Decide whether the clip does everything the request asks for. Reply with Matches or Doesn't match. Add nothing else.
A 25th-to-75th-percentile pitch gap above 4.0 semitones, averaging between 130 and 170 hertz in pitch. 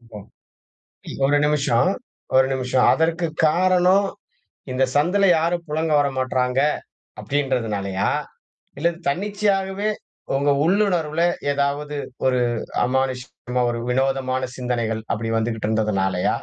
Matches